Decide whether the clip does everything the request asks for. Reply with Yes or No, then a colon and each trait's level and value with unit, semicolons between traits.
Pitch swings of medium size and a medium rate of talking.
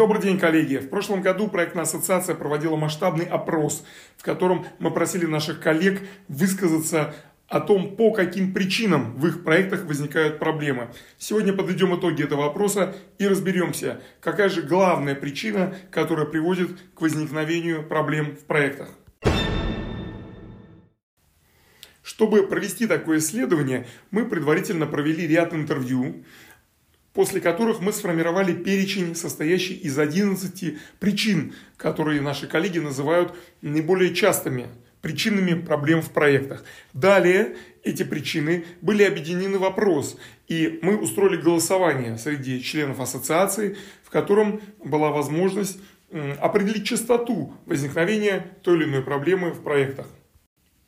Yes: average, 4.0 semitones; average, 120 wpm